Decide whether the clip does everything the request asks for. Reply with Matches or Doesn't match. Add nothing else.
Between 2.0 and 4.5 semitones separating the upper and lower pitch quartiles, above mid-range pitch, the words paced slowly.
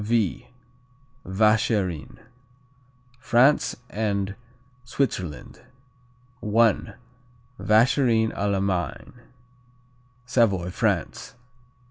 Doesn't match